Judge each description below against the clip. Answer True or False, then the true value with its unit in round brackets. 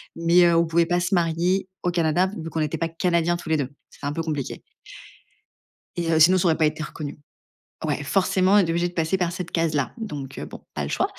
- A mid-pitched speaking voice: True (165 Hz)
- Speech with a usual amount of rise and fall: False (1.9 semitones)